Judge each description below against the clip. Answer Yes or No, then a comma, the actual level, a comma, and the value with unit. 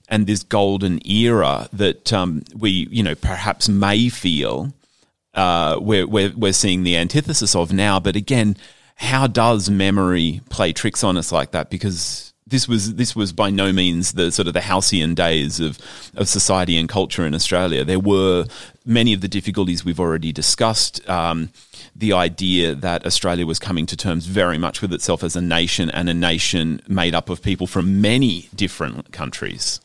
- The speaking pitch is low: Yes, very low, 95 Hz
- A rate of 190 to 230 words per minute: No, average, 180 wpm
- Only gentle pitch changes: No, average, 3.5 semitones